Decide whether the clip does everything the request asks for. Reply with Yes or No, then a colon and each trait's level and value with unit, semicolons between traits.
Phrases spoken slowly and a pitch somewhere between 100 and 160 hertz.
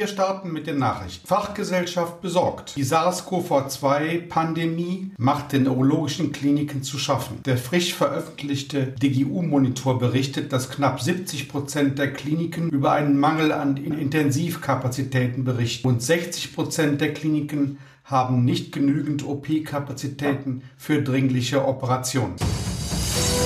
Yes: slow, 105 wpm; medium, 140 Hz